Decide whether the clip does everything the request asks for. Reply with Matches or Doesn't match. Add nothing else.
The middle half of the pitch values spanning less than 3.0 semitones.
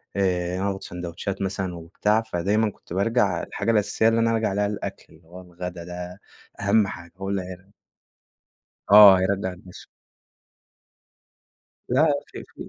Matches